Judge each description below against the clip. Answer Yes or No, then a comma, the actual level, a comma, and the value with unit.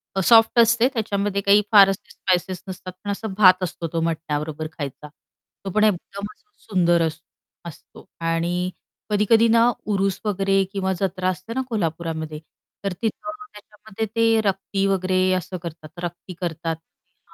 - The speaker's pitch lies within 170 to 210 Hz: Yes, high, 190 Hz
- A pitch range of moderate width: Yes, average, 3.7 semitones